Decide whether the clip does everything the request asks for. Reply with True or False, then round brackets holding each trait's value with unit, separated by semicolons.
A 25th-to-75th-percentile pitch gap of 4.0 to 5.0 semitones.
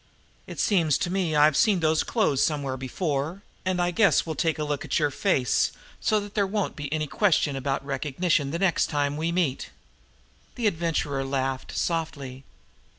True (4.3 semitones)